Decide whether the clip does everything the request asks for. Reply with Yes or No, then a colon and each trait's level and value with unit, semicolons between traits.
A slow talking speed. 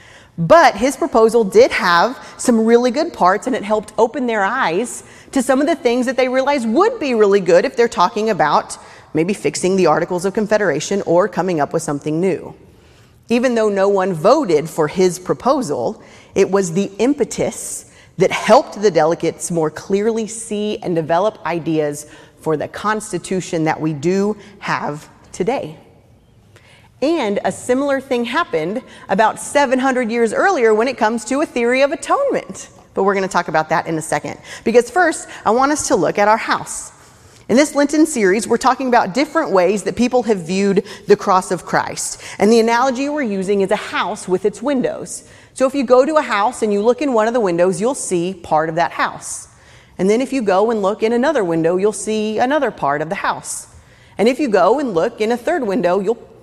No: average, 200 wpm